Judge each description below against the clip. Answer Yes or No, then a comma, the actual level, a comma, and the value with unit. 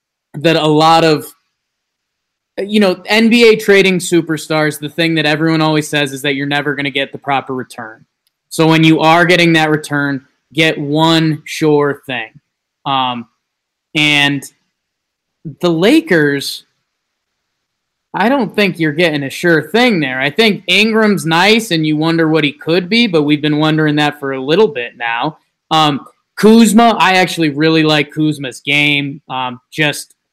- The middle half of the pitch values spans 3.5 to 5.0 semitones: No, average, 2.8 semitones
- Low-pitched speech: No, medium, 155 Hz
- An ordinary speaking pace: Yes, average, 160 wpm